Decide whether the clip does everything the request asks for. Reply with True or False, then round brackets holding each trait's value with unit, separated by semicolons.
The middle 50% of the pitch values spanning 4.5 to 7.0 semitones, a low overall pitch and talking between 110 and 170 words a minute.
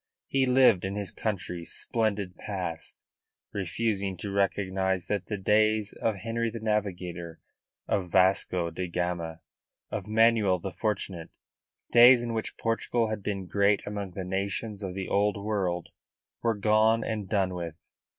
False (2.9 semitones; 100 Hz; 150 wpm)